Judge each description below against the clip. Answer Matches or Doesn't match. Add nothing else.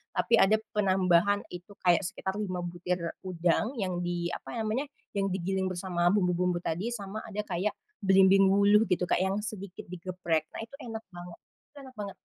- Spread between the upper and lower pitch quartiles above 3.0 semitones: Doesn't match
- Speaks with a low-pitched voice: Doesn't match